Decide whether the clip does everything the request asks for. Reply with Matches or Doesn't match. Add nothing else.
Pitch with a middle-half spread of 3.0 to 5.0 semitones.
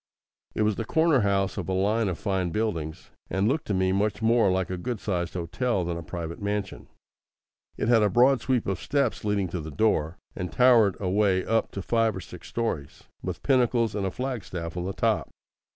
Matches